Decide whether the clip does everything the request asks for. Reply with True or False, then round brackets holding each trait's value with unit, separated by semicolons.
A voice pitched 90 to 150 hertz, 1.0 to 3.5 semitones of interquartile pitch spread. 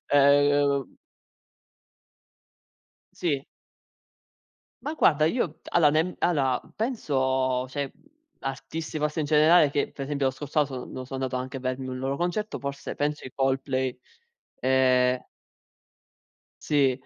True (140 Hz; 2.4 semitones)